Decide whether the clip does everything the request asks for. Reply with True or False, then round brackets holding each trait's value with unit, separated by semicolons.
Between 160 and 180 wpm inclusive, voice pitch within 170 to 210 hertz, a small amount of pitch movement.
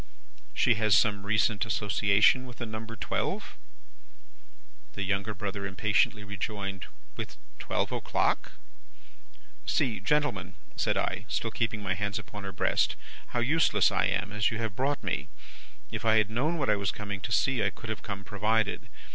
False (165 wpm; 105 Hz; 2.3 semitones)